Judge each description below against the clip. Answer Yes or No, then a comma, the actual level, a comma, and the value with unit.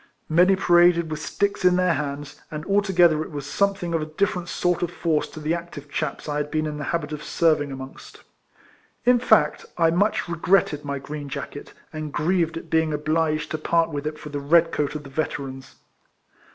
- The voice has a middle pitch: Yes, medium, 155 Hz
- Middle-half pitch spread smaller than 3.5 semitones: Yes, narrow, 2.6 semitones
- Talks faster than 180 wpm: Yes, fast, 205 wpm